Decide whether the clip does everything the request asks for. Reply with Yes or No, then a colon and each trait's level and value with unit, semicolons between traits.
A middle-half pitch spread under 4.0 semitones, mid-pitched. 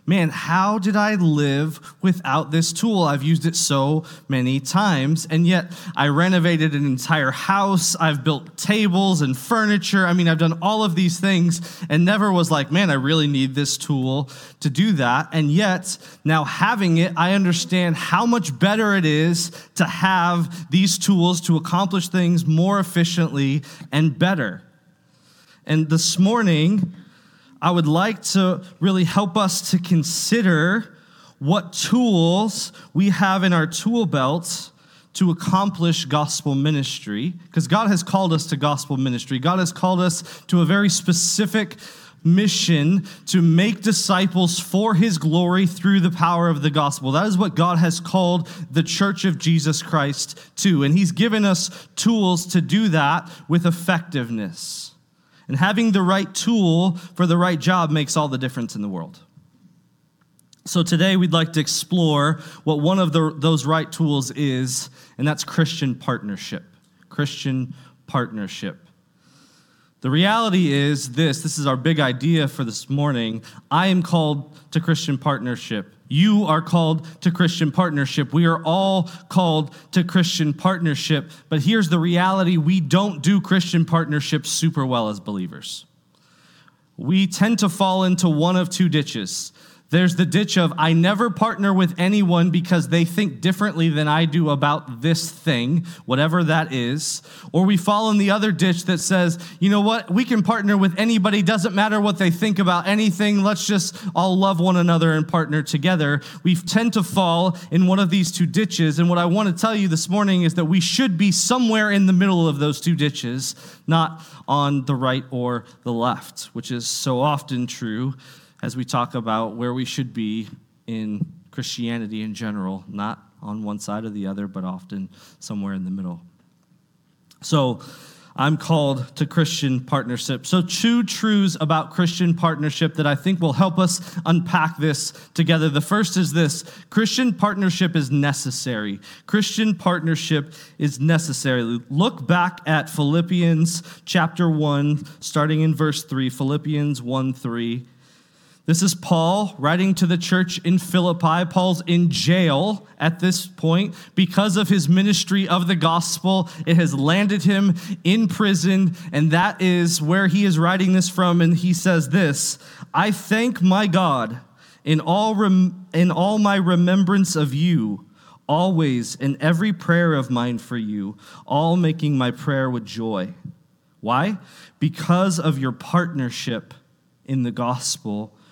Yes: average, 3.6 semitones; medium, 170 Hz